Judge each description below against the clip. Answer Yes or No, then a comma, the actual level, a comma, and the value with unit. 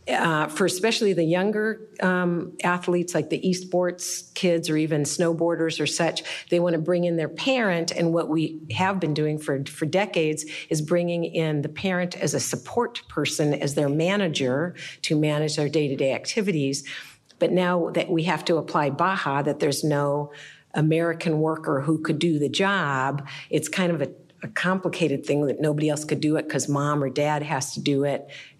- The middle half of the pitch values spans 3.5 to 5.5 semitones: No, average, 3.1 semitones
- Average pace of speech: Yes, average, 185 wpm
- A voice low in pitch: No, medium, 160 Hz